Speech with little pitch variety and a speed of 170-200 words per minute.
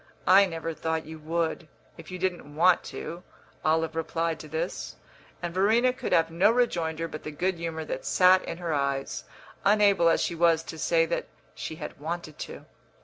Yes: narrow, 2.2 semitones; average, 185 wpm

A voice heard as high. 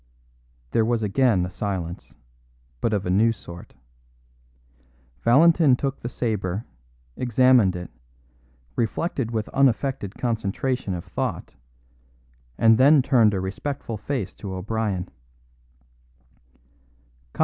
No: low, 115 Hz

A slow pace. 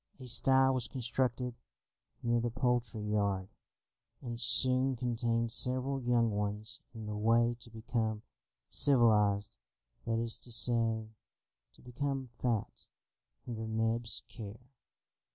Yes: slow, 115 wpm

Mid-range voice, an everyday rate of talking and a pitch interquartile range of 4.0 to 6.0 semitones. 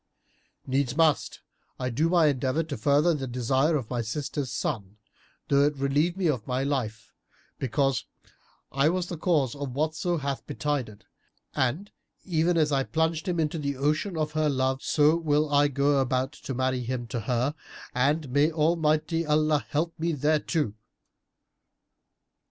No: medium, 145 Hz; average, 155 wpm; average, 3.1 semitones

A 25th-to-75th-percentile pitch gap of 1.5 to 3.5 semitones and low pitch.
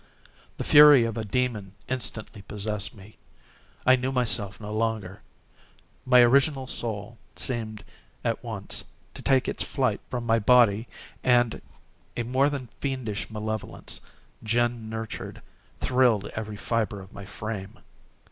Yes: average, 3.0 semitones; low, 115 Hz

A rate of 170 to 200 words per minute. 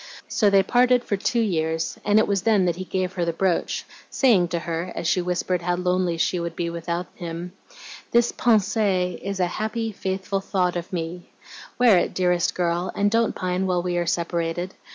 Yes: average, 195 wpm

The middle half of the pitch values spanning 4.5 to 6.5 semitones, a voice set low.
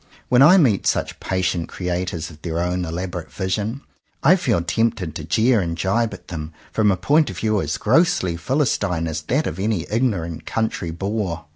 Yes: average, 5.1 semitones; very low, 95 Hz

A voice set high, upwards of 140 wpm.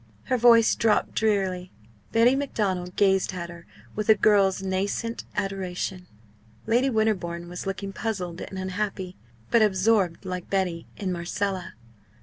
No: high, 195 Hz; slow, 135 wpm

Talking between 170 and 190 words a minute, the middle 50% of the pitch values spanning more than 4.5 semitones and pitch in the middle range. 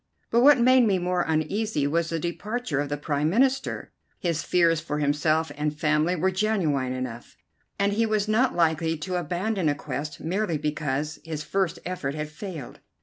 Yes: average, 175 wpm; average, 4.9 semitones; medium, 165 Hz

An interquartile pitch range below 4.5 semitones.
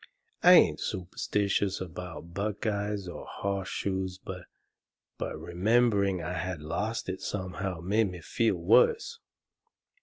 Yes: narrow, 2.4 semitones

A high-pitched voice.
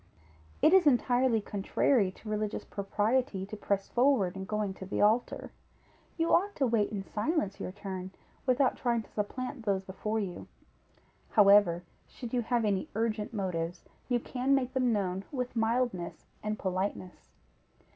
Yes: high, 215 Hz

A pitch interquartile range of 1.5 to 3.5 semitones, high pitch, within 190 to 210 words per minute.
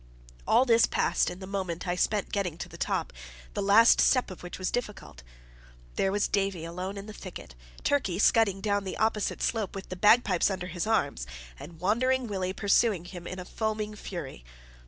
Yes: average, 3.0 semitones; high, 195 Hz; average, 195 wpm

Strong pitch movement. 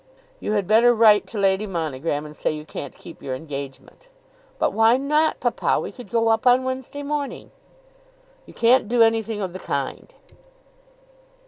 Yes: wide, 6.9 semitones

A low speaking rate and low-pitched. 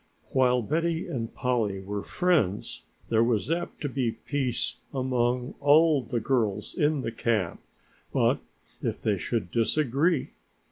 Yes: slow, 130 wpm; low, 125 Hz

